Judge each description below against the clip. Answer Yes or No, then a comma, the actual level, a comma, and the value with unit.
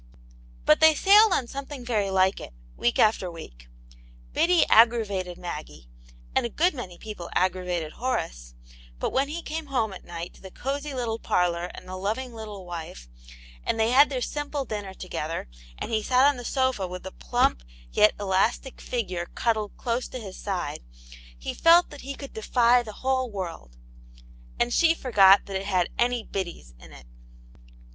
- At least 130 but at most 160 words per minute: No, average, 175 wpm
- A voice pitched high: Yes, high, 215 Hz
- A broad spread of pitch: Yes, wide, 6.2 semitones